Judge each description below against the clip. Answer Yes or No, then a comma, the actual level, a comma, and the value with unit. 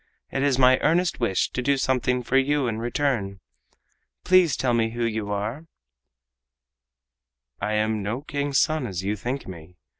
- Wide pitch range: No, average, 4.7 semitones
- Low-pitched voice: Yes, low, 125 Hz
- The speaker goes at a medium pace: Yes, average, 160 wpm